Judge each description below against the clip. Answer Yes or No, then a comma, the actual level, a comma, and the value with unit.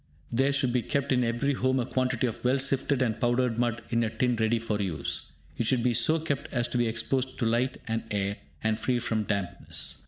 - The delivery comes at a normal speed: No, fast, 225 wpm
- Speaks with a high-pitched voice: No, low, 120 Hz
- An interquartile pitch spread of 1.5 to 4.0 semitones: Yes, narrow, 2.5 semitones